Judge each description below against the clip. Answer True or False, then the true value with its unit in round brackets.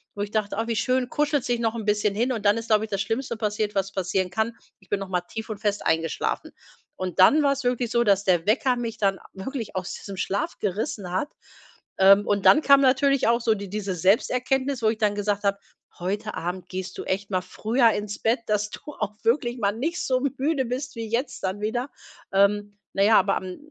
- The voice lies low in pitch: False (210 Hz)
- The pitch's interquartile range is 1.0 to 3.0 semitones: False (3.5 semitones)